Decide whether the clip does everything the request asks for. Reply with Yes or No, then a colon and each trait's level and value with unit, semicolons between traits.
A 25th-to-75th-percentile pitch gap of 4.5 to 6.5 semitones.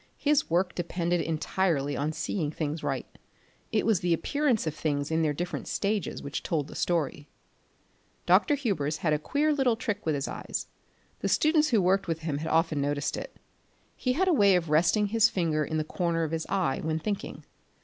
Yes: average, 5.2 semitones